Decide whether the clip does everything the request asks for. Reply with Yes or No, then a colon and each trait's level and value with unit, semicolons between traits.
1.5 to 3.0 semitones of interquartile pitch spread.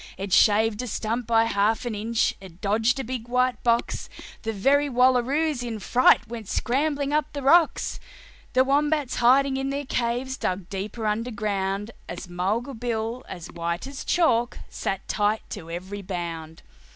No: average, 4.3 semitones